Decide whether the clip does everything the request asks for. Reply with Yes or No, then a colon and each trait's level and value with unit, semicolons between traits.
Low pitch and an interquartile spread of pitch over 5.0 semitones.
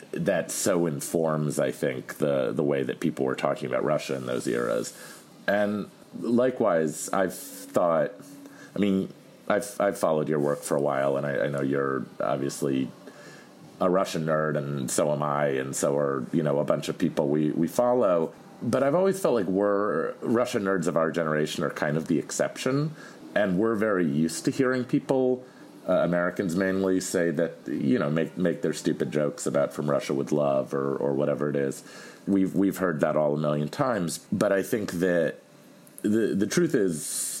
Yes: very low, 85 Hz; wide, 5.6 semitones